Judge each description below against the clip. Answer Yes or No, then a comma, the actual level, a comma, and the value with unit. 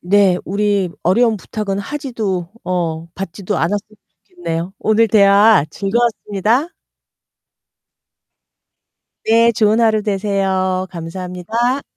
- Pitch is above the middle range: Yes, high, 200 Hz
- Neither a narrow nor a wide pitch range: Yes, average, 3.1 semitones